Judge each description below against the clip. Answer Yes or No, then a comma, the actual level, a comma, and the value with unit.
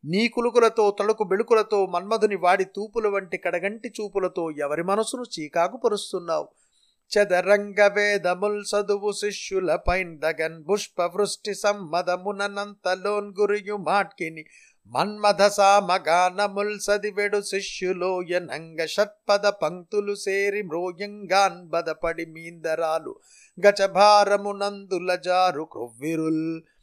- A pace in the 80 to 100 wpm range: No, slow, 70 wpm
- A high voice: Yes, high, 200 Hz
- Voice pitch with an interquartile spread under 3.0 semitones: Yes, narrow, 2.5 semitones